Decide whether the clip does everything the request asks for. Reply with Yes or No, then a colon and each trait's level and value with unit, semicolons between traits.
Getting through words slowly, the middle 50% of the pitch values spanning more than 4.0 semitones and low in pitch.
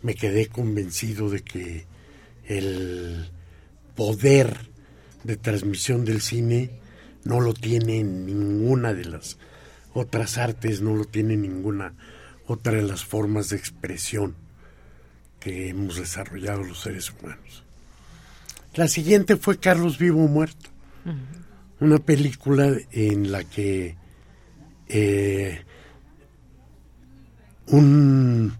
Yes: slow, 105 wpm; average, 4.7 semitones; low, 105 Hz